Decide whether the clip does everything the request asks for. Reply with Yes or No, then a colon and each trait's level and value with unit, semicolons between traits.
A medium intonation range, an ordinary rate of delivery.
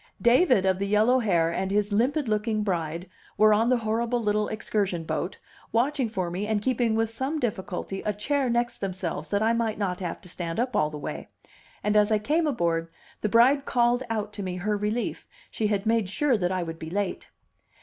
No: average, 3.9 semitones; fast, 210 wpm